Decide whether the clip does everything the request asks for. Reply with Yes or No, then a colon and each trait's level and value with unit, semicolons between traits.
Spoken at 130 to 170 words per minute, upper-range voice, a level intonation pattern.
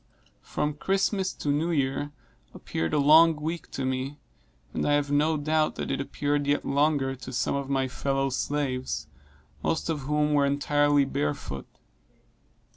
No: average, 155 wpm; medium, 145 Hz; narrow, 1.8 semitones